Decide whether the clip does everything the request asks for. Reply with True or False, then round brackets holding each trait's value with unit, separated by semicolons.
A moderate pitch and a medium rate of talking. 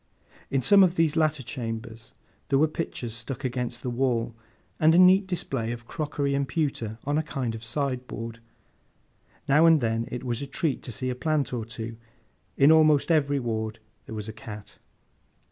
False (130 Hz; 180 wpm)